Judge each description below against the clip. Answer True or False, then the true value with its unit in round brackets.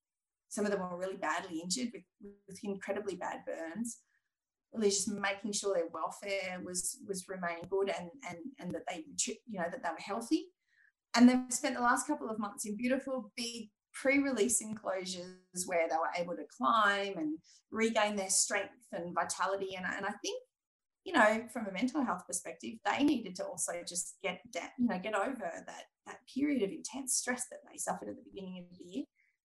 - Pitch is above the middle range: True (205 Hz)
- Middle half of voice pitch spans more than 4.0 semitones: True (5.0 semitones)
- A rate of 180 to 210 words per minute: True (200 wpm)